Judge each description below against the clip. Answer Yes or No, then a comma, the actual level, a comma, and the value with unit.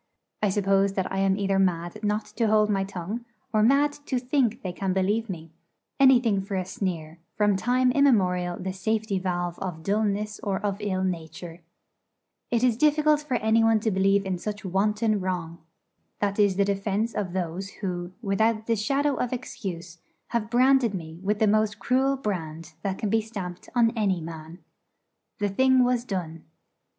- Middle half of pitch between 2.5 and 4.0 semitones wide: Yes, average, 3.4 semitones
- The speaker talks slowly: No, average, 175 wpm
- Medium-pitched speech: No, high, 200 Hz